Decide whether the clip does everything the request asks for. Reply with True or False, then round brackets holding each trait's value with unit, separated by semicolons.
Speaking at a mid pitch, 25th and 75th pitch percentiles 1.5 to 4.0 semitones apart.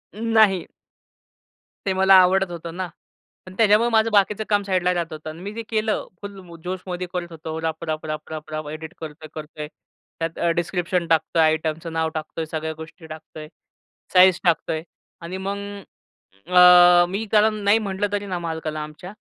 True (175 Hz; 3.4 semitones)